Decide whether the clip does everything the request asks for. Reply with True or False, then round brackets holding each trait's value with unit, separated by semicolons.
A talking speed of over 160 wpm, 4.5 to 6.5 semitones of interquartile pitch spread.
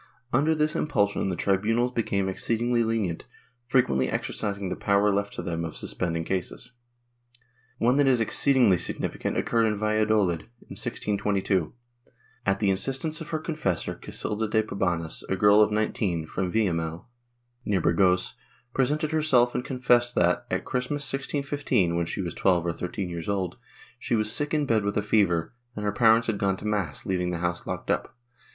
True (170 wpm; 4.9 semitones)